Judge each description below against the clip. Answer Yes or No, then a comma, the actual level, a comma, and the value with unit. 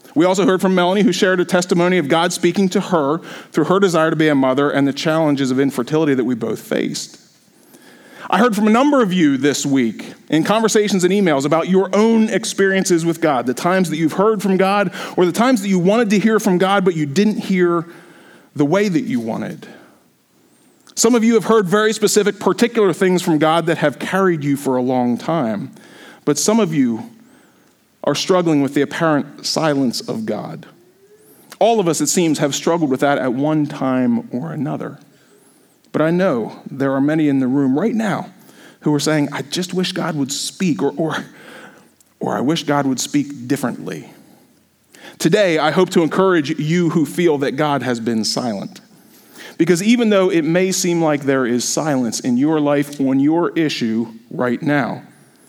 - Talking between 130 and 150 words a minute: No, average, 195 wpm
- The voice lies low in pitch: No, medium, 170 Hz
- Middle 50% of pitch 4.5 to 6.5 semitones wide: Yes, average, 5.2 semitones